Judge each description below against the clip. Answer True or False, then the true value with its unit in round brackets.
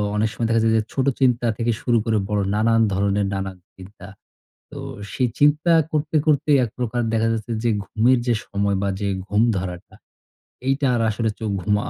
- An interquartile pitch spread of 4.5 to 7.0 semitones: False (3.4 semitones)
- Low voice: True (115 Hz)